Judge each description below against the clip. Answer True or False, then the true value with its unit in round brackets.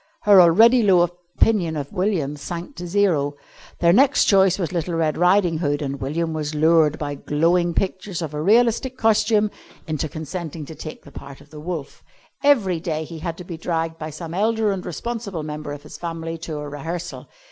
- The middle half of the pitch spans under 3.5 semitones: False (3.8 semitones)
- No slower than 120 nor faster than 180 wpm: False (190 wpm)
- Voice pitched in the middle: True (170 Hz)